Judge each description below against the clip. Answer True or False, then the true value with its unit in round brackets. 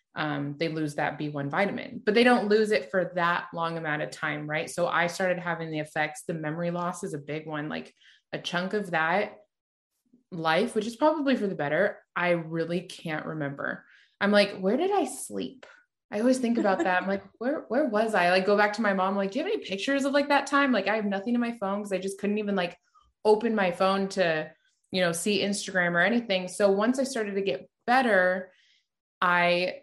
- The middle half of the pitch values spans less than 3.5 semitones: False (4.2 semitones)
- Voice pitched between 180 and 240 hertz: True (190 Hz)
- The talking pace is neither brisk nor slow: False (225 wpm)